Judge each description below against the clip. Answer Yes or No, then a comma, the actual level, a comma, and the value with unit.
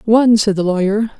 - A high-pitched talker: Yes, high, 210 Hz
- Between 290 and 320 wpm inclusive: No, average, 200 wpm